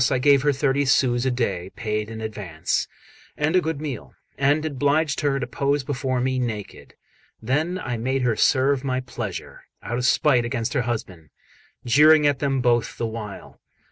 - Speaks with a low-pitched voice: Yes, low, 130 Hz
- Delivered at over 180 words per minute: No, average, 175 wpm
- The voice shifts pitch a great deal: No, average, 3.5 semitones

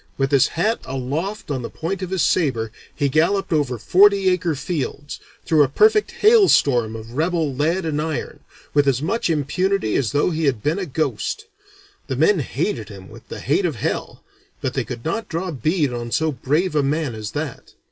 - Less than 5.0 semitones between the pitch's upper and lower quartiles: No, wide, 5.5 semitones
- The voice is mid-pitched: Yes, medium, 150 Hz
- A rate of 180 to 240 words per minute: Yes, average, 195 wpm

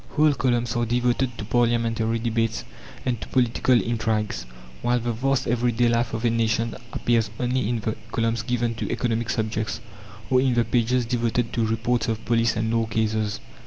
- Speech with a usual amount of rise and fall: No, narrow, 1.4 semitones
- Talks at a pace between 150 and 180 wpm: Yes, average, 175 wpm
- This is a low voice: Yes, low, 115 Hz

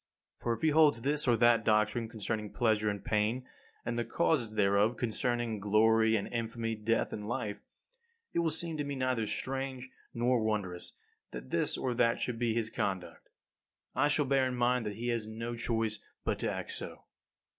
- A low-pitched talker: Yes, low, 115 Hz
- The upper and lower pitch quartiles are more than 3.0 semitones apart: No, narrow, 2.6 semitones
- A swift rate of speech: No, average, 185 wpm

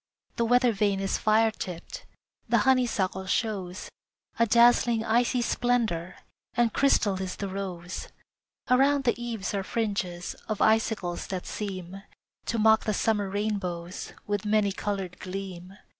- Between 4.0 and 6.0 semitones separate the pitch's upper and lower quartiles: No, average, 3.6 semitones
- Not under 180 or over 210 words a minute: No, slow, 135 wpm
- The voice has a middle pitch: No, high, 205 Hz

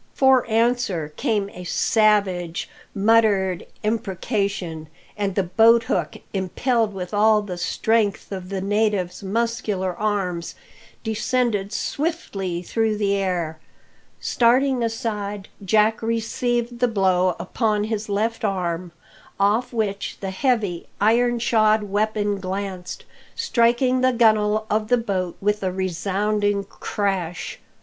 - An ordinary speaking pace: No, slow, 115 wpm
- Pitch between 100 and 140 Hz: No, high, 210 Hz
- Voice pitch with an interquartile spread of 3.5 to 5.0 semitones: No, average, 3.1 semitones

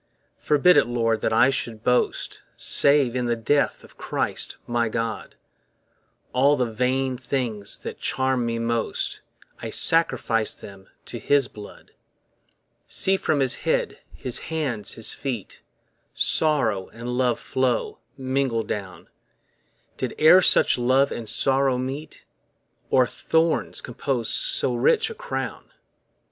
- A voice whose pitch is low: Yes, low, 125 Hz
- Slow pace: Yes, slow, 130 wpm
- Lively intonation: No, average, 3.4 semitones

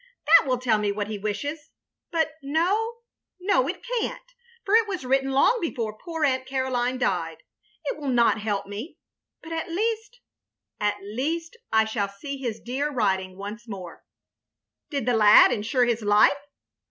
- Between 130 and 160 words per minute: No, average, 180 wpm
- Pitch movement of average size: No, wide, 7.1 semitones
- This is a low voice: No, very high, 260 Hz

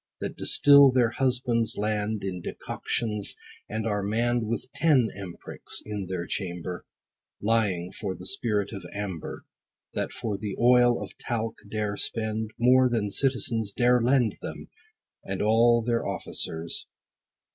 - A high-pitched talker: No, low, 110 Hz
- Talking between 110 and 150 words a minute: Yes, average, 140 wpm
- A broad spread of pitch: No, average, 2.9 semitones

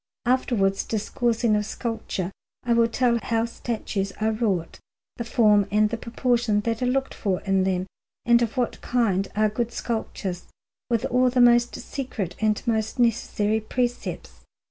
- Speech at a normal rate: Yes, average, 155 wpm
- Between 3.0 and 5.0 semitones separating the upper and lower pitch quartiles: No, narrow, 2.5 semitones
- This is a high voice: Yes, high, 225 Hz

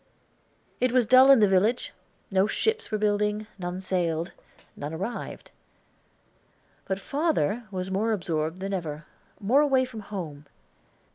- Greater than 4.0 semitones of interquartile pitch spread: Yes, average, 5.0 semitones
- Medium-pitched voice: No, high, 200 Hz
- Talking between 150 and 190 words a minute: No, slow, 135 wpm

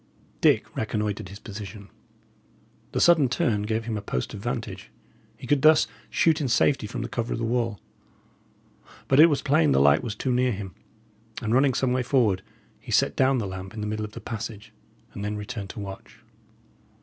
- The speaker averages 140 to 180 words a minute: No, average, 195 wpm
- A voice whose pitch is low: Yes, low, 110 Hz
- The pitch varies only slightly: No, average, 3.7 semitones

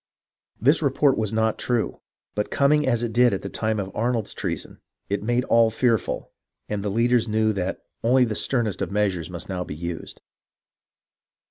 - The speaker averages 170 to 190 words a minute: Yes, average, 175 wpm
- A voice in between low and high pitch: No, low, 110 Hz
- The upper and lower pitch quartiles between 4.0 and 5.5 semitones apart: No, average, 3.3 semitones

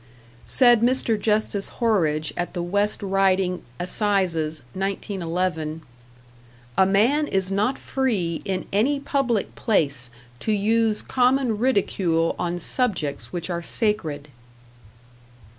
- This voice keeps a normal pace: No, slow, 110 wpm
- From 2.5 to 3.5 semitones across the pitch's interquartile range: No, average, 4.6 semitones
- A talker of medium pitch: No, high, 195 Hz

